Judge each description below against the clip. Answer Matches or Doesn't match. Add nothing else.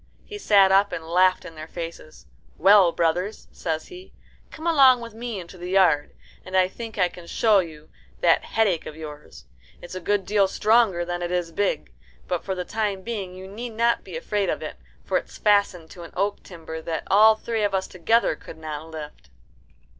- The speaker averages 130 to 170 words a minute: Doesn't match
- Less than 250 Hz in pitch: Matches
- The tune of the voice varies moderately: Matches